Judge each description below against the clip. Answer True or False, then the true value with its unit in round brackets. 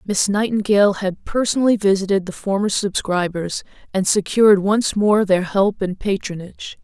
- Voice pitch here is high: True (200 Hz)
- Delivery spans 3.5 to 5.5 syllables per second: True (5.0 syllables/s)